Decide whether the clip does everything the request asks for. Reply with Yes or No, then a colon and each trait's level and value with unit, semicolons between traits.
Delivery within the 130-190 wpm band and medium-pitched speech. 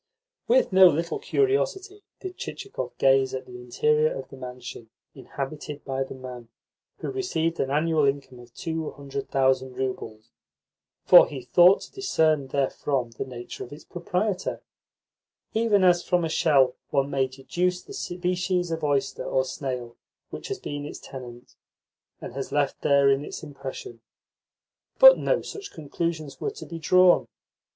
Yes: average, 155 wpm; medium, 145 Hz